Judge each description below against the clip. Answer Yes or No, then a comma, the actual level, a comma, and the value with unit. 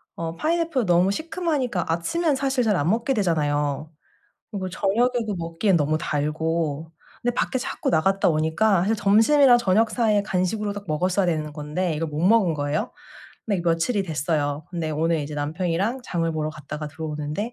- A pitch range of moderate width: No, wide, 5.9 semitones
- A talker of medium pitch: Yes, medium, 175 Hz